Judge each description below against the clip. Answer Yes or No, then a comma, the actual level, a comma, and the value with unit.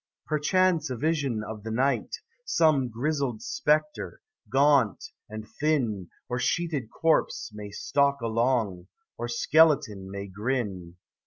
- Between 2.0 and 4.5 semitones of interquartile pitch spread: No, wide, 5.6 semitones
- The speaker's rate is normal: No, slow, 115 wpm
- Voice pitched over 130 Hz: No, low, 125 Hz